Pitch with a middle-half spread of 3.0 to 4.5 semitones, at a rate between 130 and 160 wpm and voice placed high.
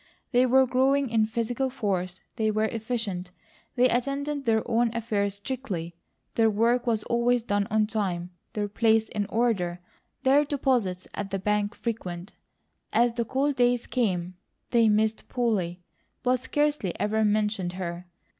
Yes: average, 3.4 semitones; average, 145 wpm; high, 220 Hz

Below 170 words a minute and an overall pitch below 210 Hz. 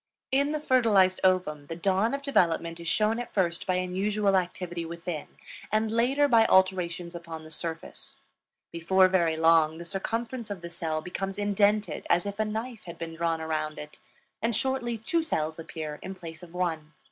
No: average, 180 wpm; medium, 185 Hz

